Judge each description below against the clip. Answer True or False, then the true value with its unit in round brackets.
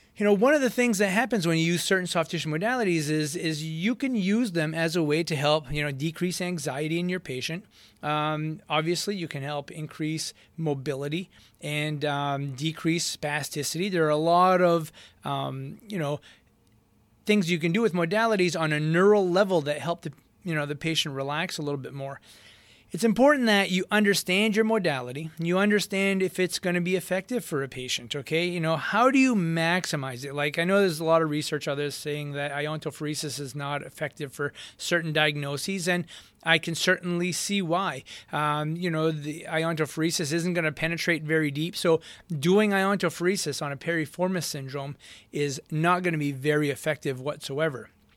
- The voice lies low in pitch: False (160 Hz)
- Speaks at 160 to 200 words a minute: True (190 wpm)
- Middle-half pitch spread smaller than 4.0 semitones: True (3.5 semitones)